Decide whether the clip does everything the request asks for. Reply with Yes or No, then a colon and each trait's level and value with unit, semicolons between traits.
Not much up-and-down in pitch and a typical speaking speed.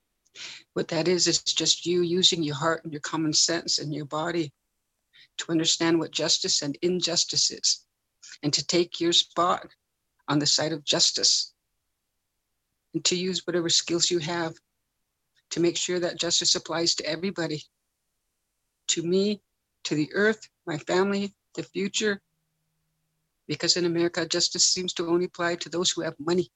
Yes: narrow, 1.9 semitones; average, 160 wpm